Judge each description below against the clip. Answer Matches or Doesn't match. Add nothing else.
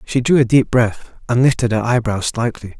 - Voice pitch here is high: Doesn't match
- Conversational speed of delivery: Doesn't match